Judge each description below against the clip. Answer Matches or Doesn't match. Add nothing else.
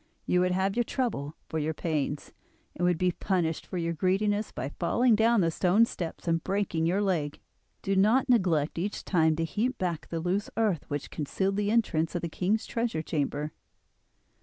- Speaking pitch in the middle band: Matches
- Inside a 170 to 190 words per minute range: Matches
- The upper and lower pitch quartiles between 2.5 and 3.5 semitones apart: Doesn't match